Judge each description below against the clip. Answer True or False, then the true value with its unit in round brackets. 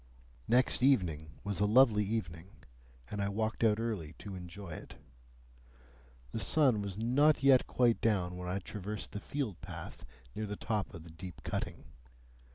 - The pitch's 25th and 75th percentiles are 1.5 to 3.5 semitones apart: False (4.2 semitones)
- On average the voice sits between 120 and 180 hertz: False (105 Hz)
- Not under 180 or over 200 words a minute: False (165 wpm)